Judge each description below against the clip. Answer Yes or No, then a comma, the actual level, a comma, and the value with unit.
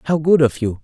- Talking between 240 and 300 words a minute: Yes, fast, 290 wpm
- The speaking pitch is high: No, medium, 140 Hz